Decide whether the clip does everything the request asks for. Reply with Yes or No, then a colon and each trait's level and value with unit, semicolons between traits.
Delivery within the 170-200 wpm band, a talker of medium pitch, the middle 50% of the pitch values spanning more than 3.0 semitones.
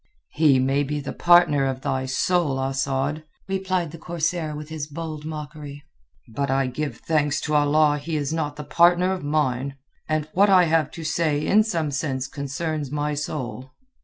No: average, 175 wpm; medium, 150 Hz; average, 2.7 semitones